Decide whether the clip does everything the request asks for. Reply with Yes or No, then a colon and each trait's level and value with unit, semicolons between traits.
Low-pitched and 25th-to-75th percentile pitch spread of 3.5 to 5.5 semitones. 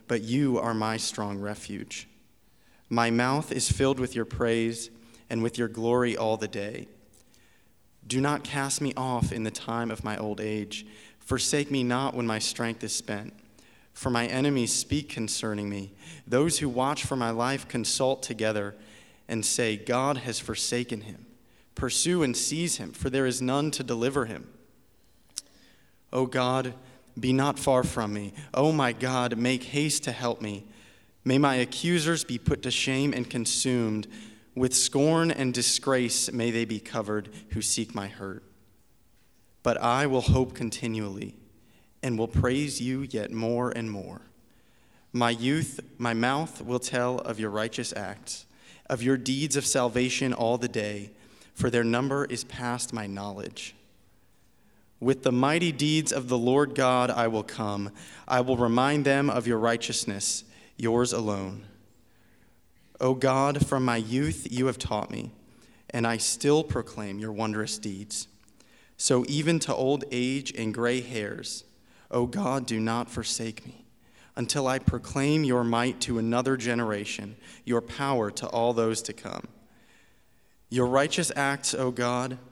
No: low, 120 Hz; average, 2.9 semitones